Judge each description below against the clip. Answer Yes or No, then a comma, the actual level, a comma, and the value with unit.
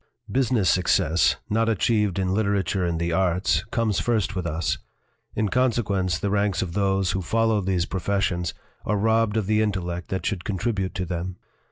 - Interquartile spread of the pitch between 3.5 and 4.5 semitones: No, average, 3.1 semitones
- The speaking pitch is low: Yes, very low, 95 Hz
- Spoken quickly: No, average, 175 wpm